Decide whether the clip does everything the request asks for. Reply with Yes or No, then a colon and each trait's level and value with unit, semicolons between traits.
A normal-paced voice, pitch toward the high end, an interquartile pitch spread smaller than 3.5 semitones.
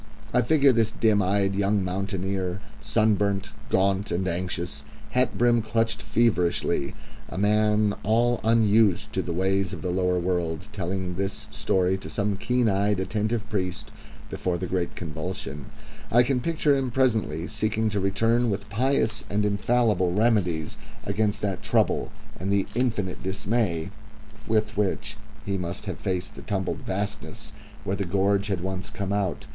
No: average, 150 wpm; low, 100 Hz; average, 2.9 semitones